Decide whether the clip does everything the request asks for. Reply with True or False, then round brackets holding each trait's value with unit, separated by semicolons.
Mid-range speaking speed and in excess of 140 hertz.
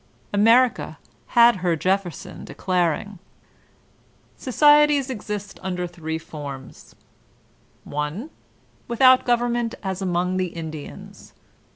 False (90 wpm; 190 Hz)